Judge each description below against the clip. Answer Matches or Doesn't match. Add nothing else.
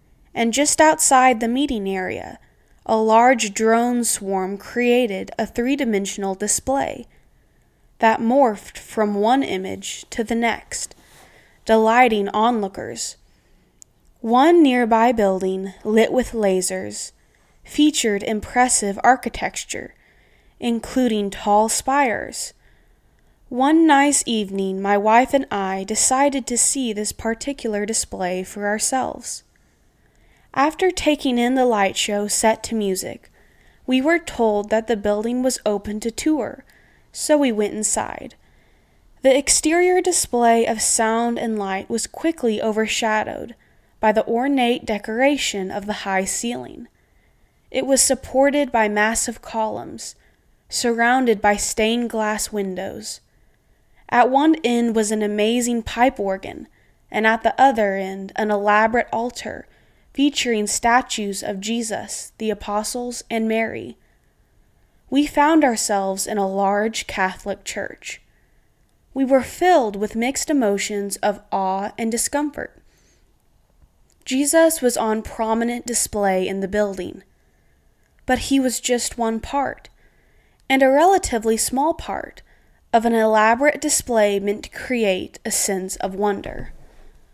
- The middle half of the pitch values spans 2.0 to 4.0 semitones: Matches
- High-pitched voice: Matches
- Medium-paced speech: Doesn't match